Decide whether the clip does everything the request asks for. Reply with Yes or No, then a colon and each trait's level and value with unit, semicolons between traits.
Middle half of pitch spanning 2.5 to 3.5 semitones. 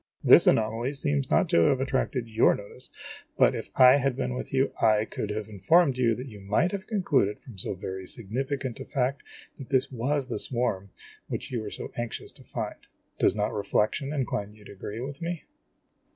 No: average, 4.5 semitones